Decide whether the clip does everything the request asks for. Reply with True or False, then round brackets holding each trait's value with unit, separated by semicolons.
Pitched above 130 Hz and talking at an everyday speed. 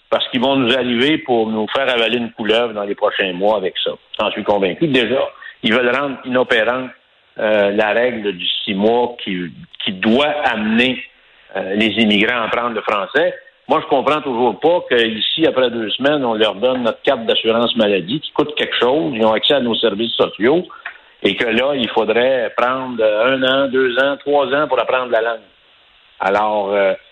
False (115 Hz; 195 wpm)